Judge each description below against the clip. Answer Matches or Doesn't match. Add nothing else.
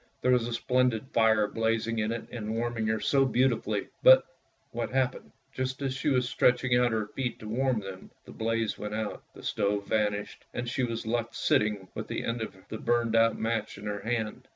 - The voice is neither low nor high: Doesn't match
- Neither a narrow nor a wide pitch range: Doesn't match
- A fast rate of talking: Matches